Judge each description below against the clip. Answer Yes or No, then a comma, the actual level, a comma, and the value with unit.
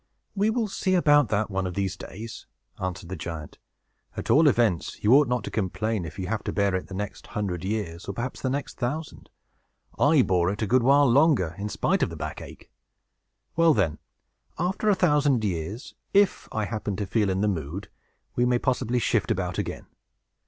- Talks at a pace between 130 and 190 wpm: No, average, 200 wpm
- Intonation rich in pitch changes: Yes, wide, 6.6 semitones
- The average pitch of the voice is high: No, low, 110 Hz